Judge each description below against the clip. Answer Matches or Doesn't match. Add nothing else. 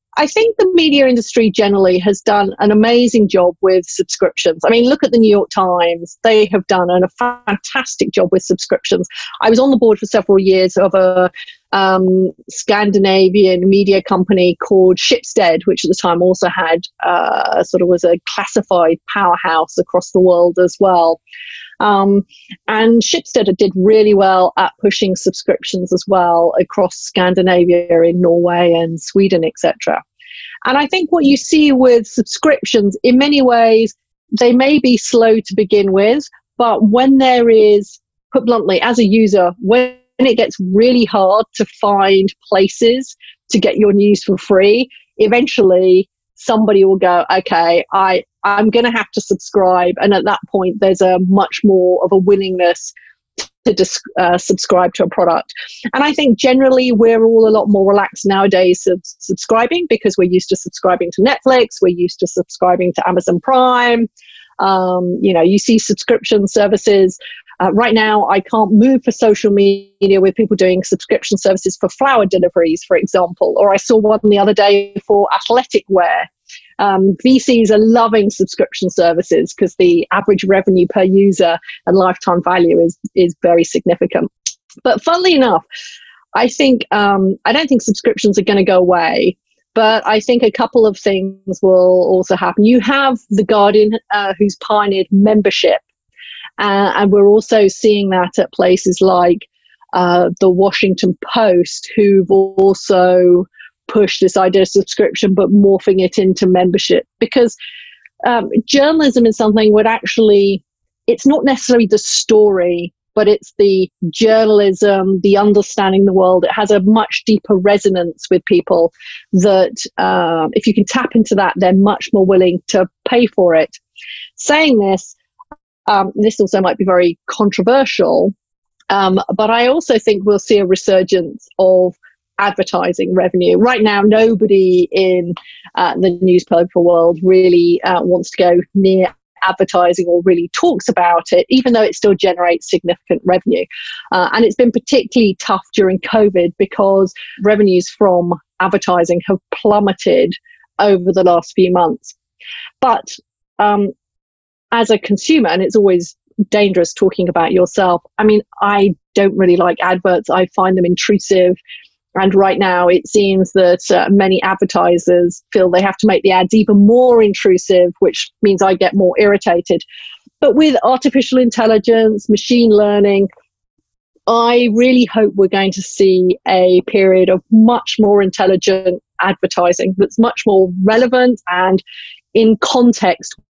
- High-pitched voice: Matches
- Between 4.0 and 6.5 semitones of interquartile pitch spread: Doesn't match